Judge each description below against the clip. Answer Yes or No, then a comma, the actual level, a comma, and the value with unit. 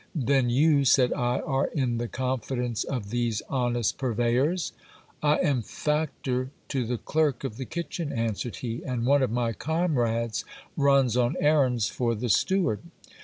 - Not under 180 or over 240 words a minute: No, average, 155 wpm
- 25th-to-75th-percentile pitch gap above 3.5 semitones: No, average, 3.1 semitones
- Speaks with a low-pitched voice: Yes, low, 125 Hz